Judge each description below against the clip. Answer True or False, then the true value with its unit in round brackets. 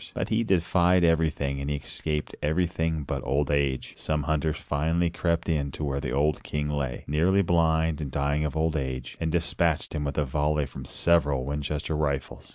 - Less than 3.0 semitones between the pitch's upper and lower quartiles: True (2.4 semitones)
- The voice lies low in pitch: True (75 Hz)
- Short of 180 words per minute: False (185 wpm)